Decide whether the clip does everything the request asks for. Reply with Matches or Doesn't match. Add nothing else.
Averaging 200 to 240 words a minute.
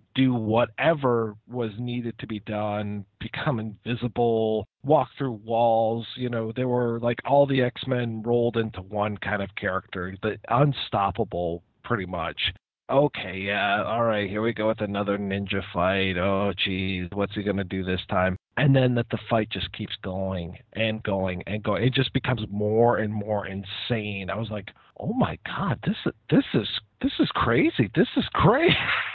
Doesn't match